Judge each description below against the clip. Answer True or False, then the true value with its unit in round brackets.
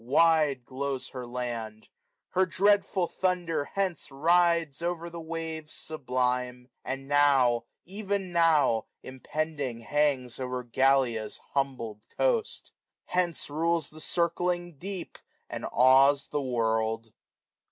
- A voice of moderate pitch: True (145 Hz)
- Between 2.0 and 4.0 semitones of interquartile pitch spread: False (5.2 semitones)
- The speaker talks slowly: True (115 wpm)